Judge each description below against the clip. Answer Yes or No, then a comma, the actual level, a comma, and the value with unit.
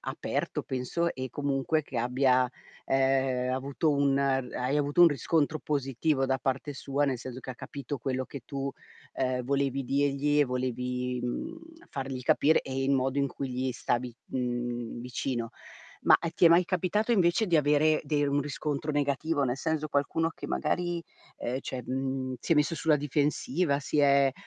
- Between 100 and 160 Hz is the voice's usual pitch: Yes, medium, 140 Hz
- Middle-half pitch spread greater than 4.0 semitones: No, narrow, 2.4 semitones